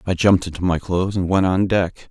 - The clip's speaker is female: No, male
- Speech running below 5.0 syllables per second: No, 6.1 syllables/s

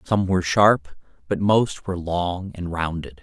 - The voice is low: Yes, very low, 90 Hz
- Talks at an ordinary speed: Yes, average, 165 wpm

